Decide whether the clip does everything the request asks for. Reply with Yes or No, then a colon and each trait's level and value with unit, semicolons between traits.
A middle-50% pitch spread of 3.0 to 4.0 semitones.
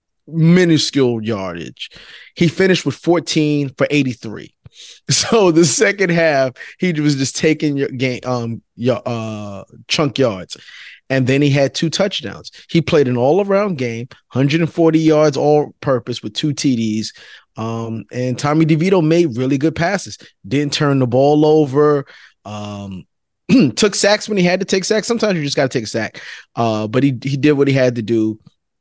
No: average, 4.9 semitones